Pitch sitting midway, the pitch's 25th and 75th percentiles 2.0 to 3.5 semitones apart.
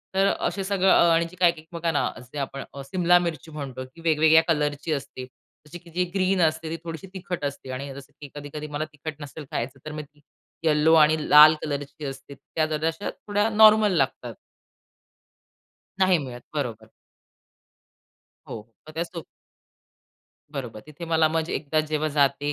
Yes: medium, 155 Hz; average, 3.0 semitones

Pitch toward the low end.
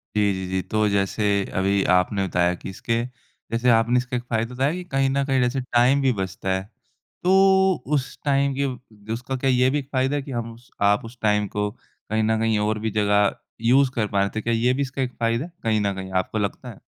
Yes: low, 115 Hz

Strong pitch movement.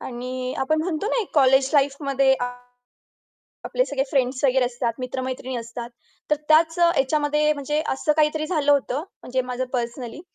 No: average, 2.9 semitones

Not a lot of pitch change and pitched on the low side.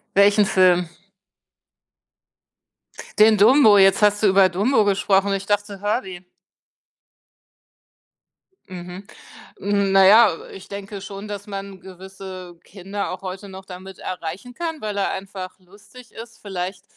No: narrow, 1.5 semitones; high, 195 Hz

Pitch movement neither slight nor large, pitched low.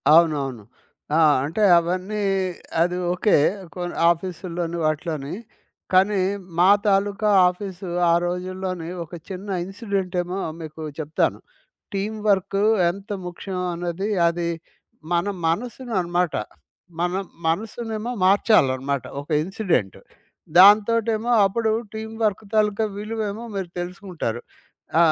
No: average, 3.4 semitones; medium, 185 Hz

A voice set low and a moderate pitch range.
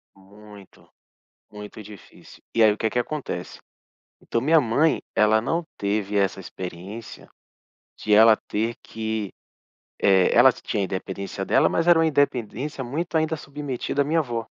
No: low, 110 Hz; wide, 5.8 semitones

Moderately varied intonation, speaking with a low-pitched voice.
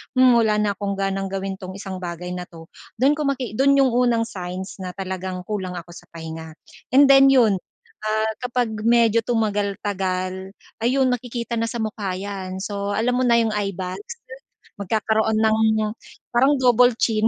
No: average, 4.0 semitones; high, 215 Hz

